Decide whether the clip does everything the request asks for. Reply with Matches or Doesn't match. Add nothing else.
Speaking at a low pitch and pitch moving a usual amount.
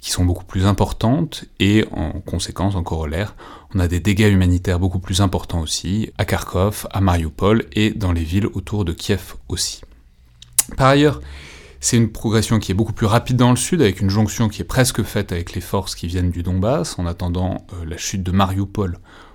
Matches